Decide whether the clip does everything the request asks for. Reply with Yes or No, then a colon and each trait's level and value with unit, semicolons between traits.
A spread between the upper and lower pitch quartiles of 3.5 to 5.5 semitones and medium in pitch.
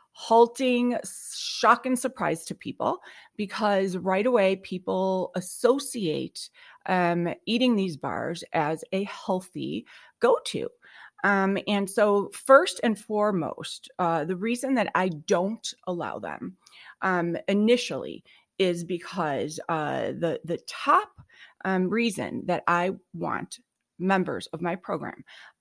No: average, 5.1 semitones; high, 195 Hz